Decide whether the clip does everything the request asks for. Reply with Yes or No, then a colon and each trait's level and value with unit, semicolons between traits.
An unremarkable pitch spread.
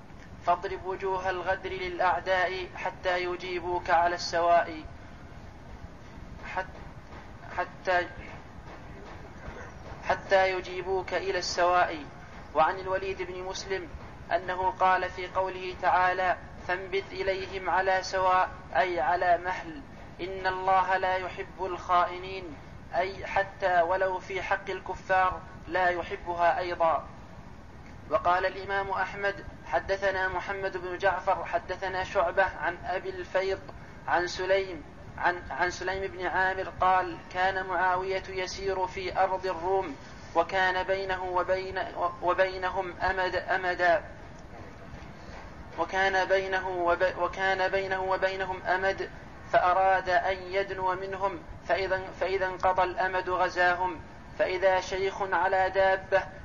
No: narrow, 1.1 semitones